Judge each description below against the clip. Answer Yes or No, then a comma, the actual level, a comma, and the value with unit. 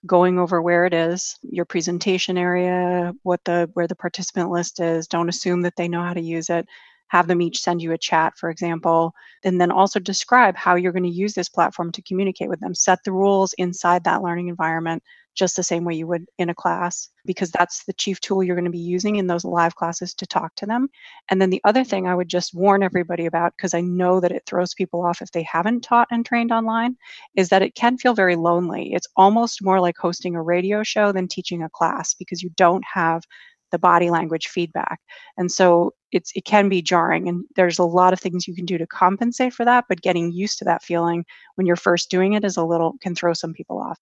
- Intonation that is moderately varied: No, narrow, 1.8 semitones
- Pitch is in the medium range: Yes, medium, 180 Hz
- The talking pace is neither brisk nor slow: No, fast, 235 wpm